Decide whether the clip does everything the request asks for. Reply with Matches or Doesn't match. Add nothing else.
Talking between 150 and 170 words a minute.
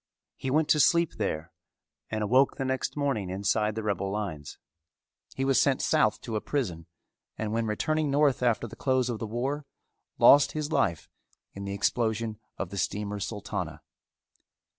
Matches